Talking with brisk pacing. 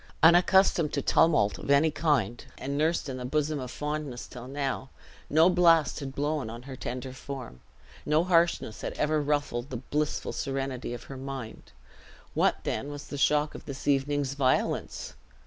No: average, 165 wpm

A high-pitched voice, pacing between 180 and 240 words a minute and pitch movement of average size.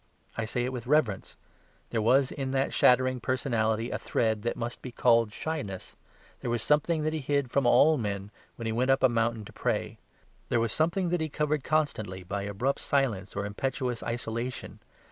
No: low, 120 Hz; average, 190 wpm; average, 3.9 semitones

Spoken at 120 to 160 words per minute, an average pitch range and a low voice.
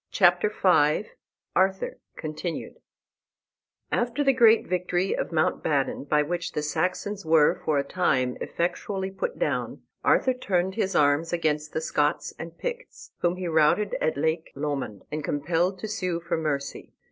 No: average, 150 wpm; average, 4.1 semitones; medium, 170 Hz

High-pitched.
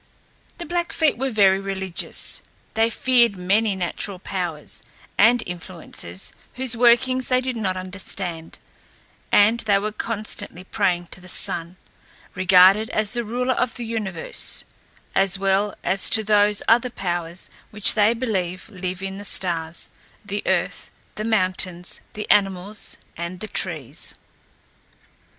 Yes: high, 195 Hz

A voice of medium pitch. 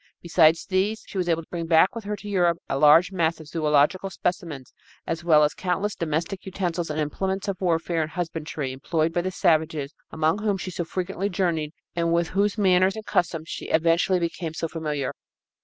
Yes: medium, 170 Hz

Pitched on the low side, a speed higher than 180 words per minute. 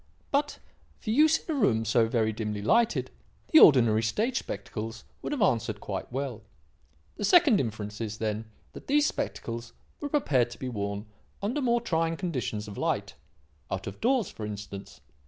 No: low, 120 Hz; average, 170 wpm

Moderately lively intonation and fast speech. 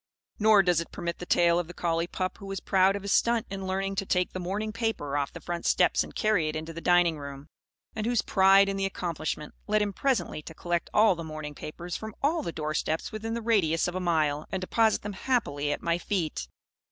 Yes: average, 3.9 semitones; fast, 240 wpm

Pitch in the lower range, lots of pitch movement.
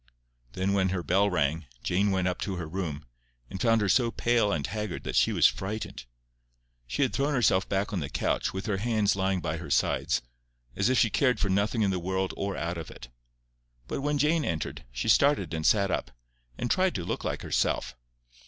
No: very low, 95 Hz; average, 4.2 semitones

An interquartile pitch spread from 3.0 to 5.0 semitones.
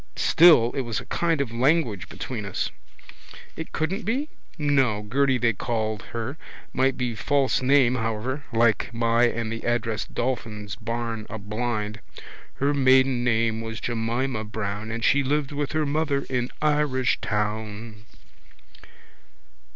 Yes: average, 3.7 semitones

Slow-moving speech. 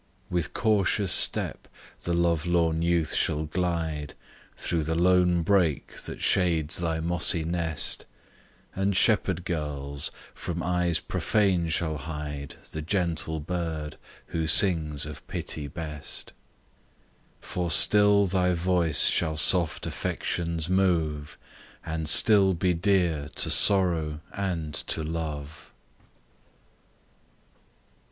Yes: slow, 110 wpm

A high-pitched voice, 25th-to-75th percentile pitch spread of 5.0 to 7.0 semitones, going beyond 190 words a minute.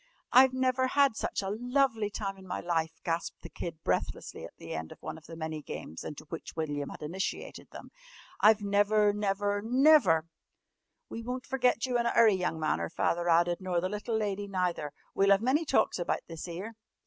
Yes: high, 200 Hz; wide, 5.5 semitones; fast, 205 wpm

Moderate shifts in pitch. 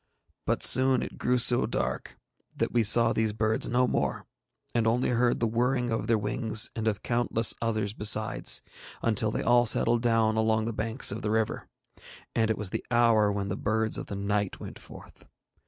No: narrow, 1.6 semitones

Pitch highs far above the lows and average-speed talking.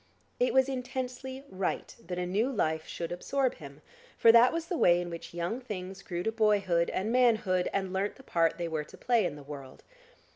No: wide, 6.3 semitones; fast, 210 wpm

